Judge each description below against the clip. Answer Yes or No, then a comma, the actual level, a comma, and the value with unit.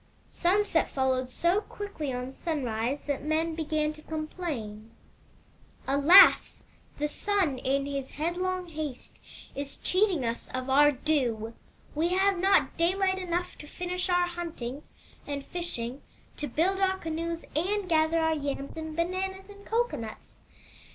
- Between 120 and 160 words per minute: Yes, slow, 135 wpm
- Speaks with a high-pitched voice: Yes, very high, 315 Hz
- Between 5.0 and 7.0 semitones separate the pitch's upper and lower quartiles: No, average, 4.6 semitones